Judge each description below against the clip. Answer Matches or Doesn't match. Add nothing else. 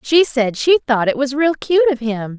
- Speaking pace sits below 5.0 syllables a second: Matches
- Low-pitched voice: Doesn't match